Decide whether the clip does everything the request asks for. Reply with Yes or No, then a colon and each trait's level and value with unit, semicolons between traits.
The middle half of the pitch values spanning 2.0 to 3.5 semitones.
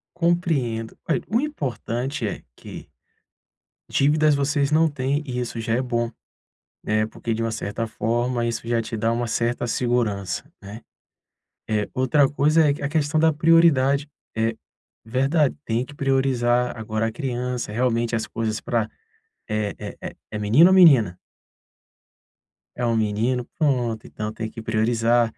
No: average, 3.9 semitones